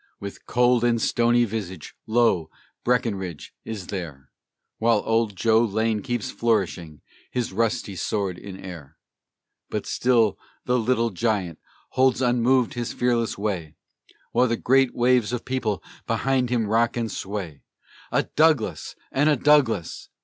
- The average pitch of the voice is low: Yes, low, 115 Hz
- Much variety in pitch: No, average, 3.9 semitones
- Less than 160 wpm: Yes, average, 140 wpm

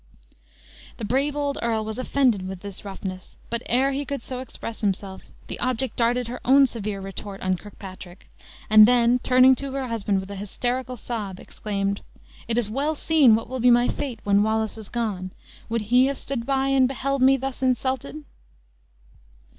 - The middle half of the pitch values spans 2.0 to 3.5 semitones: No, average, 4.2 semitones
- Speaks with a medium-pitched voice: No, high, 235 Hz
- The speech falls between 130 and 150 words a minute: No, average, 180 wpm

